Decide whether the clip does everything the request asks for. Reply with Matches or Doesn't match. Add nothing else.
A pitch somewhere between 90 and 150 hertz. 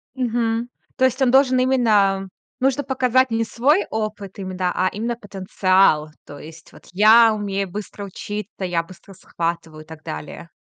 Doesn't match